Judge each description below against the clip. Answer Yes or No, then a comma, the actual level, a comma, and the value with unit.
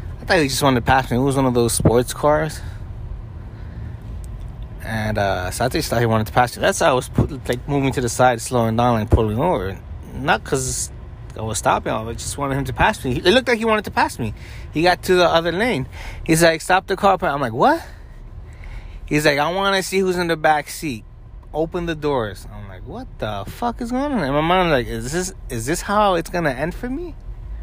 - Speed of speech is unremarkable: No, fast, 240 wpm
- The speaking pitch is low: Yes, low, 125 Hz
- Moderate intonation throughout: No, wide, 7.3 semitones